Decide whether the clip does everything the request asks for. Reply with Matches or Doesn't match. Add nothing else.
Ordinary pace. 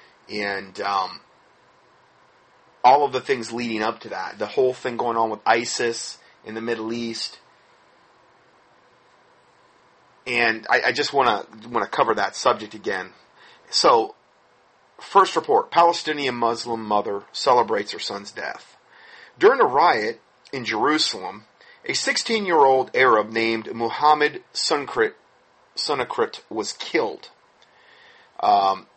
Doesn't match